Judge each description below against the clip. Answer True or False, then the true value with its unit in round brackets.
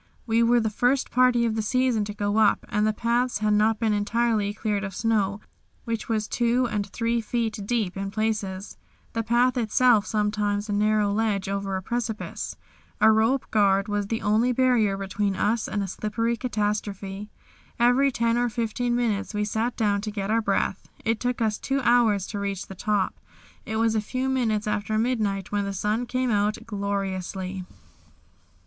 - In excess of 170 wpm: True (180 wpm)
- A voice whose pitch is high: True (215 Hz)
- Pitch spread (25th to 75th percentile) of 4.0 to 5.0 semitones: False (2.4 semitones)